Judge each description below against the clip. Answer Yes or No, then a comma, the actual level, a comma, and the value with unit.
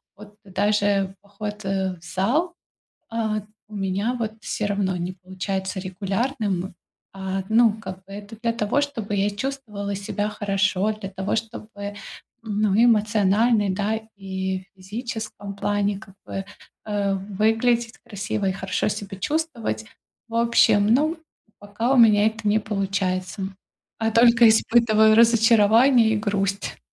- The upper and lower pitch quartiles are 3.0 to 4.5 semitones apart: No, narrow, 2.4 semitones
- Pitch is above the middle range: Yes, high, 205 Hz